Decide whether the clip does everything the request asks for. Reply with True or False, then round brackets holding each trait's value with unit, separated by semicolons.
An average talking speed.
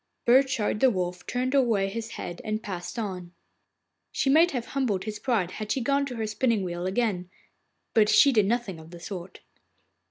True (185 wpm)